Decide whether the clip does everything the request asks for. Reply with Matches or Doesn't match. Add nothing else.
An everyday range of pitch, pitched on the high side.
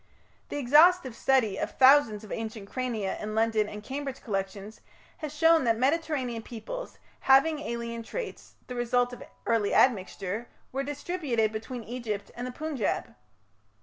Matches